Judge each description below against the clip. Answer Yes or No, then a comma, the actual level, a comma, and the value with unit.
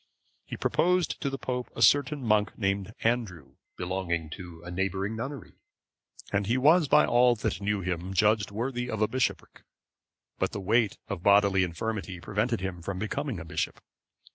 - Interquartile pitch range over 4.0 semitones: Yes, average, 4.6 semitones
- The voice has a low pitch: Yes, low, 105 Hz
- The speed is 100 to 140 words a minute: No, average, 165 wpm